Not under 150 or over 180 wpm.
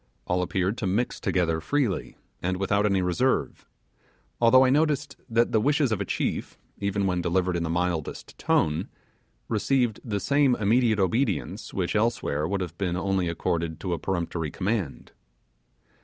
Yes: average, 155 wpm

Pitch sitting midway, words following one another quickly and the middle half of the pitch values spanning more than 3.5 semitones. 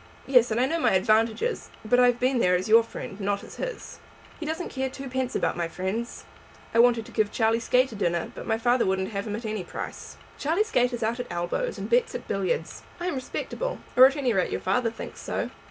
No: high, 235 Hz; fast, 235 wpm; average, 4.3 semitones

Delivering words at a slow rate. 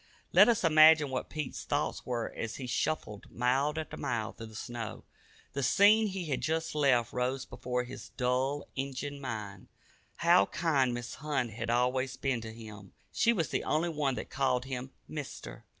No: average, 175 wpm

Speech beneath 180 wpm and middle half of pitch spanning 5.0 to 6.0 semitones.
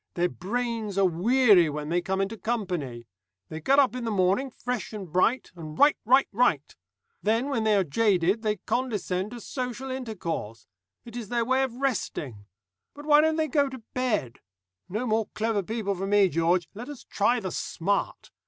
No: average, 185 wpm; wide, 5.5 semitones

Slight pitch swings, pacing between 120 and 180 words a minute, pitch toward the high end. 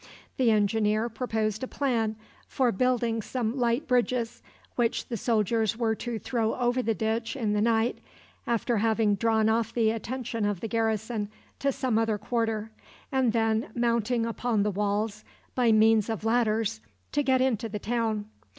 Yes: narrow, 1.7 semitones; average, 160 wpm; high, 225 Hz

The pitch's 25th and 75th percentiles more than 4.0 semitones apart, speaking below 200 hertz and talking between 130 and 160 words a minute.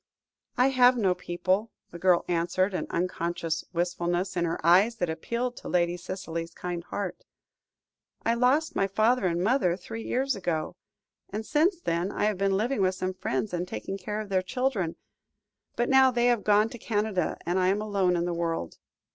No: average, 4.5 semitones; high, 190 Hz; average, 185 wpm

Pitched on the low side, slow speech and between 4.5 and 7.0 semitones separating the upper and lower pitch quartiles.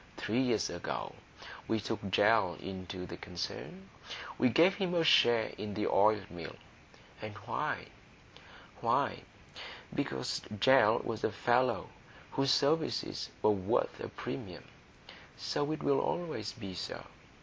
Yes: low, 110 Hz; slow, 130 wpm; wide, 5.4 semitones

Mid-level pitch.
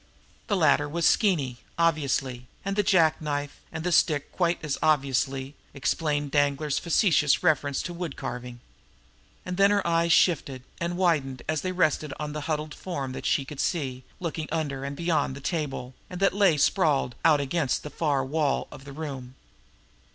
Yes: medium, 150 Hz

